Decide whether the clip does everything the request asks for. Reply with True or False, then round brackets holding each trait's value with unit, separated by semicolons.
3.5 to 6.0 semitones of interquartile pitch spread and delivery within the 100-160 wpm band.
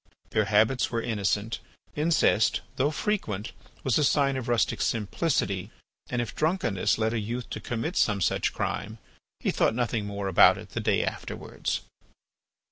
True (4.2 semitones; 155 wpm)